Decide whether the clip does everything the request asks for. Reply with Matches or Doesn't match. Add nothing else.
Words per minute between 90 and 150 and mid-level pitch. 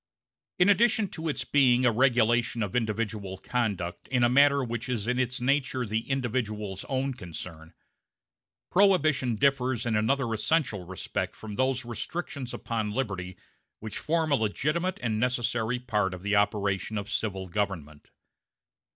Doesn't match